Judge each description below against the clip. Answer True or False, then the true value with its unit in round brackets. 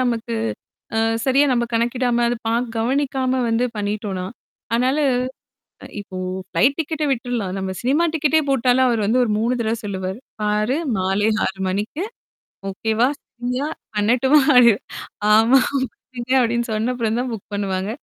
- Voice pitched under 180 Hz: False (235 Hz)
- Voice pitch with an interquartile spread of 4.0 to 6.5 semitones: False (3.5 semitones)